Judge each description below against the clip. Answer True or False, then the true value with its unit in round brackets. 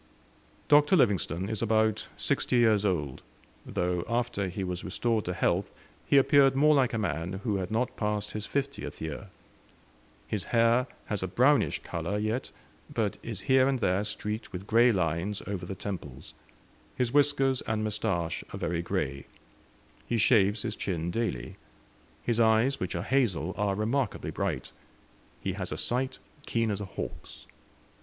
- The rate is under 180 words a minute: True (160 wpm)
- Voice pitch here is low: True (105 Hz)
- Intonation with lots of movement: False (4.6 semitones)